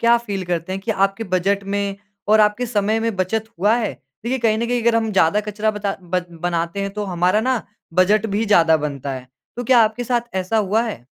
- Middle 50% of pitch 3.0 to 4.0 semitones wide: Yes, average, 3.3 semitones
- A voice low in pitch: No, high, 205 Hz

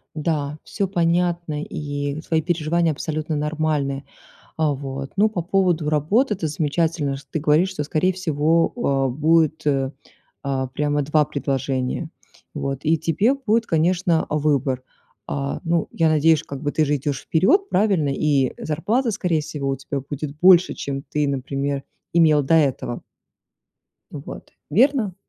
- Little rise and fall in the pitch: No, average, 3.3 semitones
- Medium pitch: Yes, medium, 155 Hz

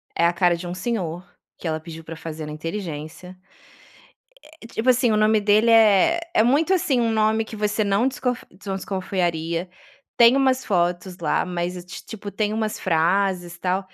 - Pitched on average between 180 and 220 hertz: Yes, high, 195 Hz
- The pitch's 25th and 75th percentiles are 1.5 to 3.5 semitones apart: No, average, 4.3 semitones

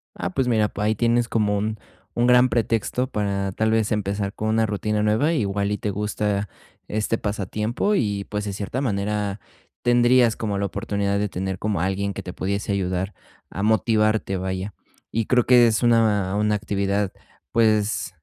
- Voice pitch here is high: No, low, 105 Hz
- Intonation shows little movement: Yes, narrow, 2.1 semitones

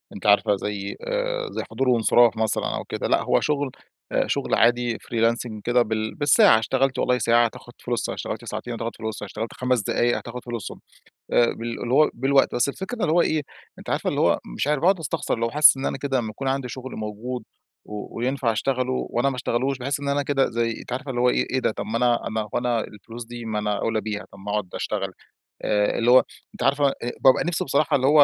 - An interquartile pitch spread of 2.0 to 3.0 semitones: No, average, 3.4 semitones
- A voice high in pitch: No, low, 120 Hz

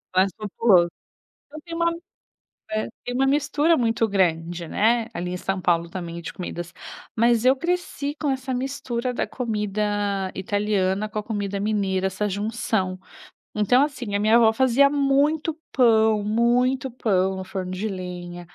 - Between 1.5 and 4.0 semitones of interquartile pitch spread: No, average, 5.0 semitones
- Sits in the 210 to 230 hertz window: Yes, high, 215 Hz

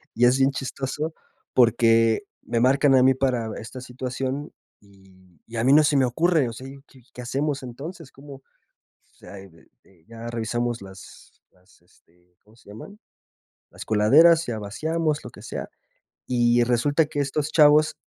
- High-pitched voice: No, low, 125 Hz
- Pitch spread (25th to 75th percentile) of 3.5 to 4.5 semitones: Yes, average, 4.2 semitones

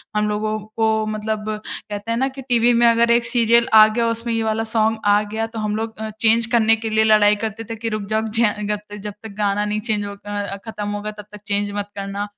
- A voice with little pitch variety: Yes, narrow, 1.5 semitones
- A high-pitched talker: Yes, high, 215 Hz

